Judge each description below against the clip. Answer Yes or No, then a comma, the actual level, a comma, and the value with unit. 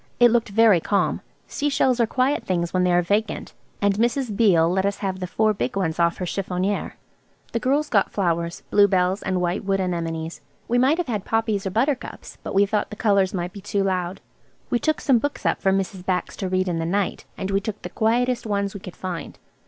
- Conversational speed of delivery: No, fast, 220 wpm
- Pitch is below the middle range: No, high, 195 Hz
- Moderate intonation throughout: Yes, average, 3.6 semitones